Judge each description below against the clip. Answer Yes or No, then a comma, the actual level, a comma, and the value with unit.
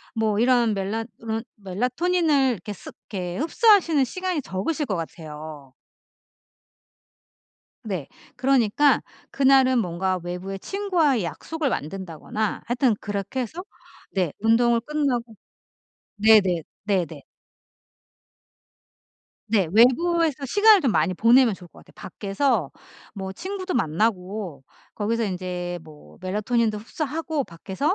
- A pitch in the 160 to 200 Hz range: No, high, 220 Hz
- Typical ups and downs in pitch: No, wide, 6.4 semitones